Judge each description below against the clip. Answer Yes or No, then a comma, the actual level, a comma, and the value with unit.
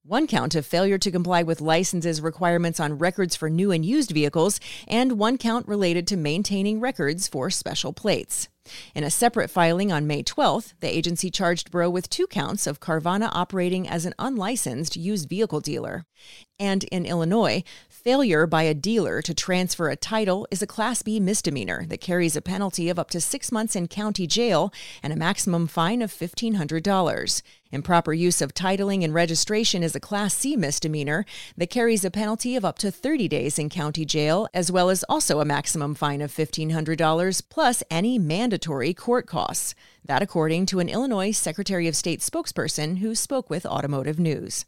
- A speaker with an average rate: Yes, average, 180 wpm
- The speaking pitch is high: No, medium, 180 Hz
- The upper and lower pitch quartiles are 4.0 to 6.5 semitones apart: Yes, average, 4.4 semitones